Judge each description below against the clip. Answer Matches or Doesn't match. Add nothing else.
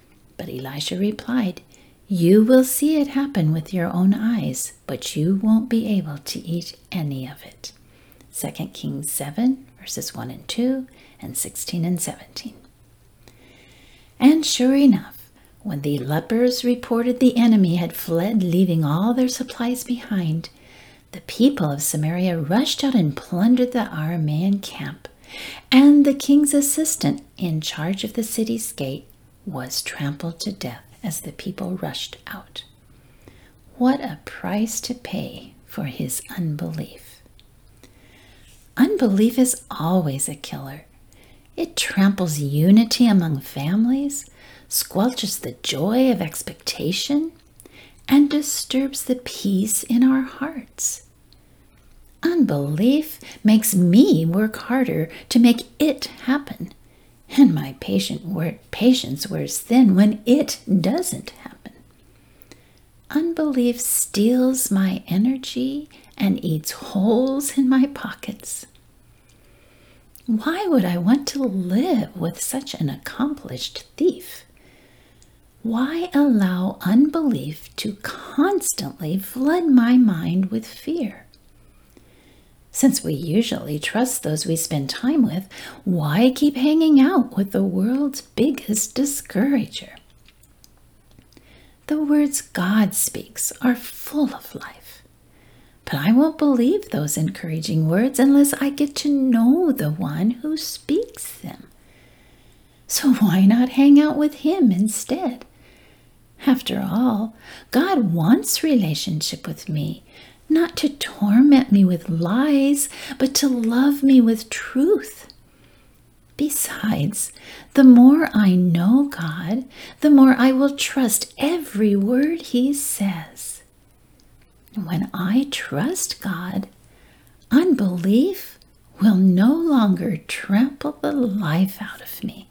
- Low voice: Doesn't match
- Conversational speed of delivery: Doesn't match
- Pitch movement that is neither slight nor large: Doesn't match